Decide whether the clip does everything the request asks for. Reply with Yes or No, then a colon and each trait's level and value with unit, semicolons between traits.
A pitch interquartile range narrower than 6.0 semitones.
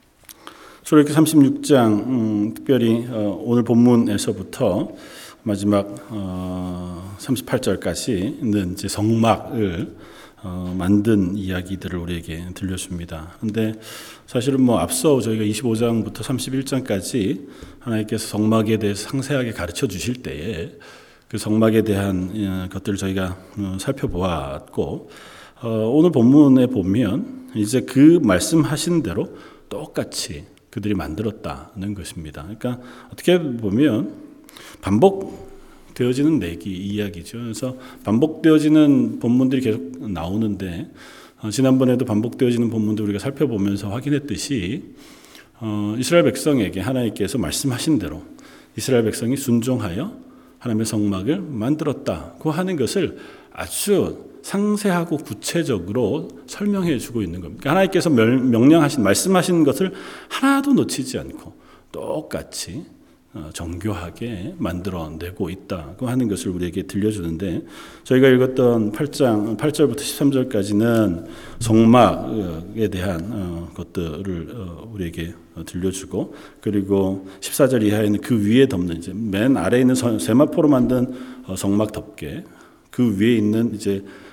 Yes: average, 5.1 semitones